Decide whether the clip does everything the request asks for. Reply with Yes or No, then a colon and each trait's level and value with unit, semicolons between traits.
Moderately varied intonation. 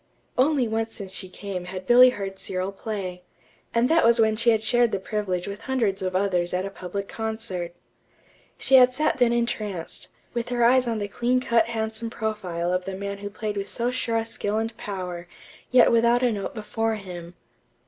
Yes: average, 3.5 semitones